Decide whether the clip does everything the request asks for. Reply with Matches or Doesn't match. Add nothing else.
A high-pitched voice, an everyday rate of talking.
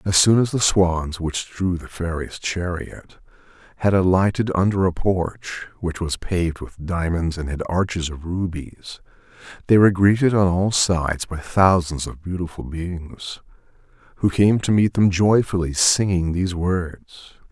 Doesn't match